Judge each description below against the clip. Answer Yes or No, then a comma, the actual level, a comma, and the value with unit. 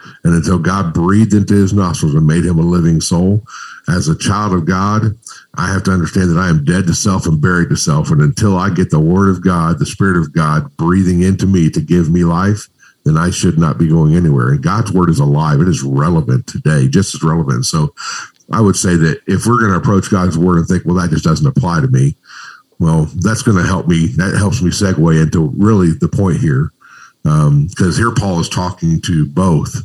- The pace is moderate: No, fast, 230 wpm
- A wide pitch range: No, average, 3.5 semitones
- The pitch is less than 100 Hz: Yes, very low, 90 Hz